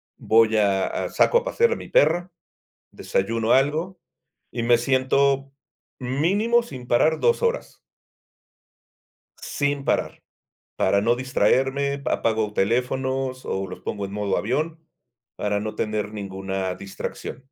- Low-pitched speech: Yes, low, 125 Hz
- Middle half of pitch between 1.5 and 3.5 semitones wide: No, average, 5.2 semitones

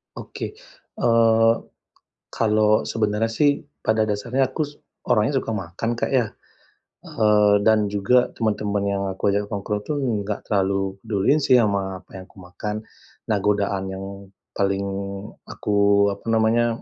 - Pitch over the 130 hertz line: No, low, 105 Hz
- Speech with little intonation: Yes, narrow, 2.1 semitones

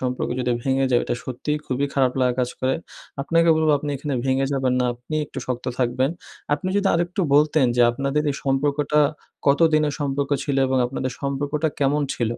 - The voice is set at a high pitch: No, low, 135 Hz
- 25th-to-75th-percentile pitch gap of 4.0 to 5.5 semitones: No, narrow, 2.4 semitones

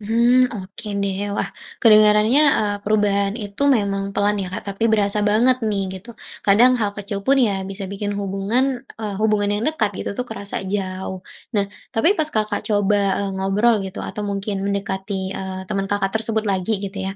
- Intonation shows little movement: Yes, narrow, 1.5 semitones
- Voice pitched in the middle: No, high, 205 Hz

